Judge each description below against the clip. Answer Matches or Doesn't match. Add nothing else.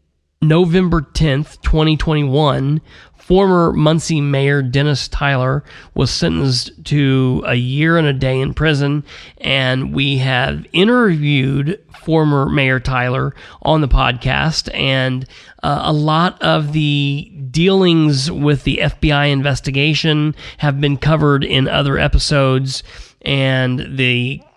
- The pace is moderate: Doesn't match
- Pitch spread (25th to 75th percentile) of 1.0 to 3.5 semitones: Matches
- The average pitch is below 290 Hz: Matches